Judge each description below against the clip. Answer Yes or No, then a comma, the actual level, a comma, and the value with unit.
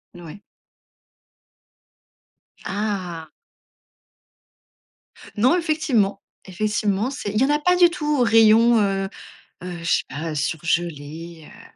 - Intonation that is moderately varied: No, wide, 5.9 semitones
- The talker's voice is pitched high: Yes, high, 205 Hz